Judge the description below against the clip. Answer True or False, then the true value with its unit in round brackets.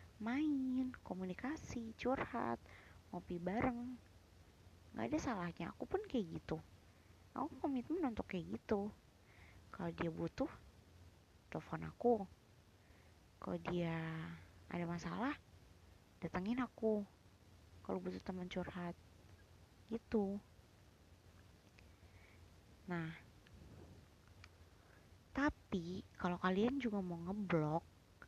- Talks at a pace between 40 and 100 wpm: True (85 wpm)